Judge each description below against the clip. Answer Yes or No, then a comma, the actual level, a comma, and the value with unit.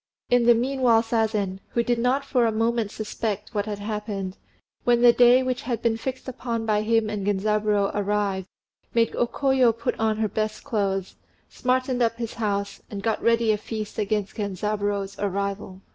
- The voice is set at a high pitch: Yes, high, 220 Hz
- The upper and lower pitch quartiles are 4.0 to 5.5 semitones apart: No, narrow, 2.5 semitones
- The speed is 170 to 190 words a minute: Yes, average, 175 wpm